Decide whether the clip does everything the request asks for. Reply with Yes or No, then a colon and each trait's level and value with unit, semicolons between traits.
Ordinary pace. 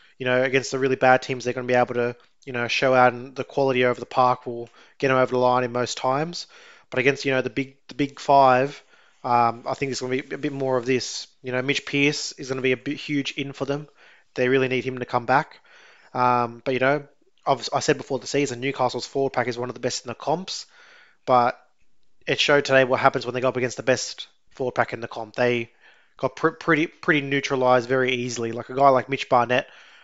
No: fast, 255 wpm